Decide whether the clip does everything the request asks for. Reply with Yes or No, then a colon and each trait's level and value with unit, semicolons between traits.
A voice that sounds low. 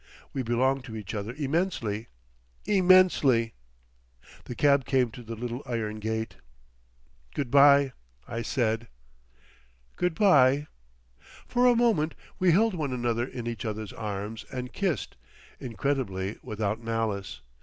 Yes: low, 120 Hz